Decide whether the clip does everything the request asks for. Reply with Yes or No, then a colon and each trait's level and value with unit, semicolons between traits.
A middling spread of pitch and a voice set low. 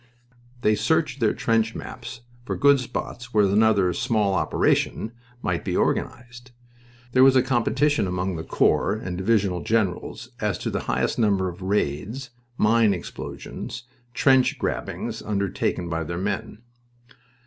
Yes: average, 4.4 semitones; low, 110 Hz